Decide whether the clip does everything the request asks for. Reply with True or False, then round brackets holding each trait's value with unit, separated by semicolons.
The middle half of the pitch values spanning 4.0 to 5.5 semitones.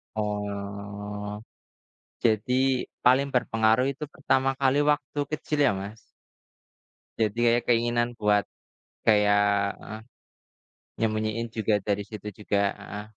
False (2.7 semitones)